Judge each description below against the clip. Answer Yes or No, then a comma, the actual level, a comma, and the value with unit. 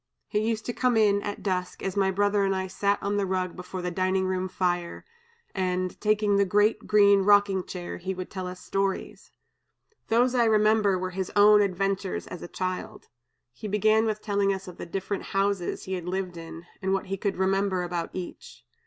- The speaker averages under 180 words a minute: No, average, 200 wpm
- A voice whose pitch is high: Yes, high, 195 Hz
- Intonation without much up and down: Yes, narrow, 1.8 semitones